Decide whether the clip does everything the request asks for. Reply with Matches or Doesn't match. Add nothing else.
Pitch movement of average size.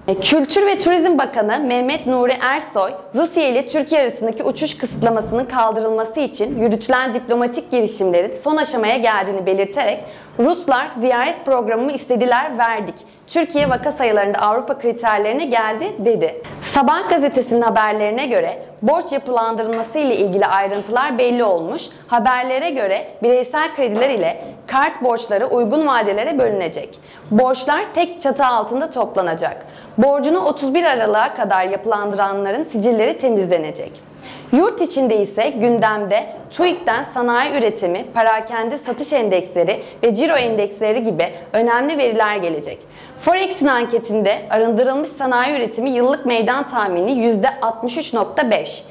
Matches